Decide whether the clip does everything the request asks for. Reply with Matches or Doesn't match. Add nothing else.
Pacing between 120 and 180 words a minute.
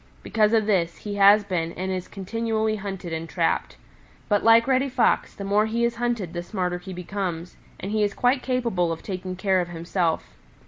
Doesn't match